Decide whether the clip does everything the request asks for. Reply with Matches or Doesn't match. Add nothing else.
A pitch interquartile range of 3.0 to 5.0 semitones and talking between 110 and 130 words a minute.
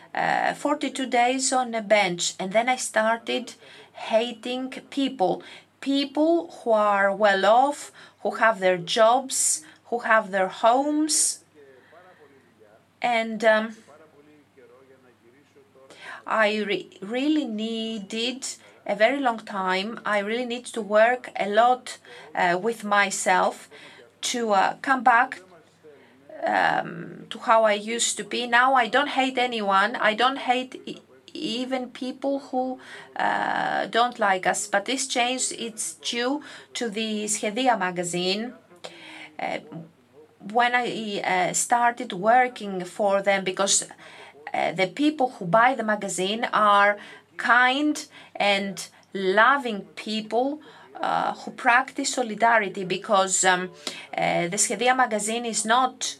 Matches